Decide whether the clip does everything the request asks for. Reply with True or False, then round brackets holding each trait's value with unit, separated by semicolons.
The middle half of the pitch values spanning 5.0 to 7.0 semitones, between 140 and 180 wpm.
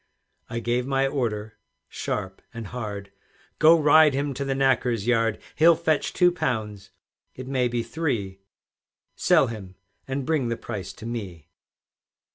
False (4.5 semitones; 145 wpm)